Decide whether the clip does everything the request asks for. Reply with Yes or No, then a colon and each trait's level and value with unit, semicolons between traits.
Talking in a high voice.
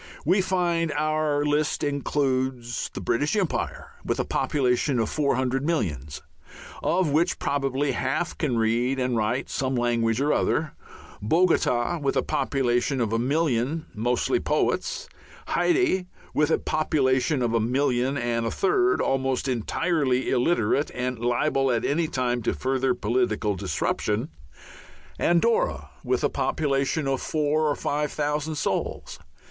No: low, 135 Hz